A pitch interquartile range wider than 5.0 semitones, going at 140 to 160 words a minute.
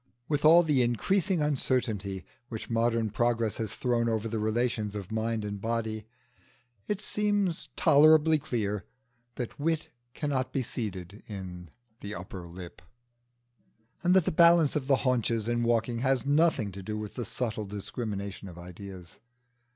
Yes: wide, 5.6 semitones; average, 150 wpm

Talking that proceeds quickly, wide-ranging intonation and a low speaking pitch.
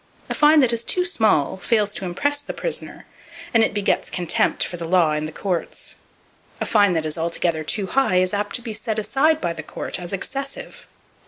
No: fast, 210 wpm; wide, 5.9 semitones; high, 205 Hz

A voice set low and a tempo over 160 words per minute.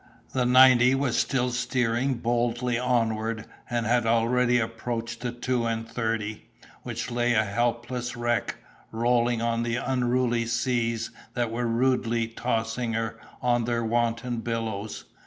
No: low, 120 Hz; slow, 135 wpm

